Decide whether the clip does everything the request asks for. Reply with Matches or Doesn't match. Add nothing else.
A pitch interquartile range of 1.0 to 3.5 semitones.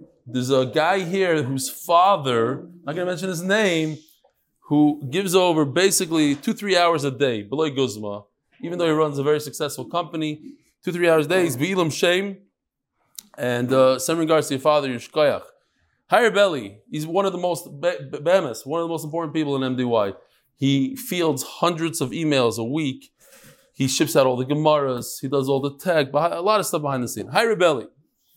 Doesn't match